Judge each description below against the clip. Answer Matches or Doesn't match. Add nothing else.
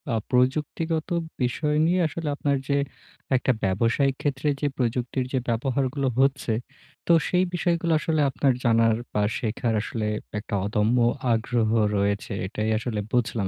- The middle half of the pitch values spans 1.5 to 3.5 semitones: Doesn't match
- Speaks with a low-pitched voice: Matches